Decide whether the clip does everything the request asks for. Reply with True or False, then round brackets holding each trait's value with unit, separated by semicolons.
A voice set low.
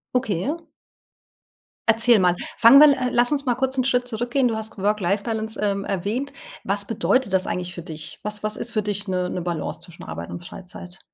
False (210 Hz)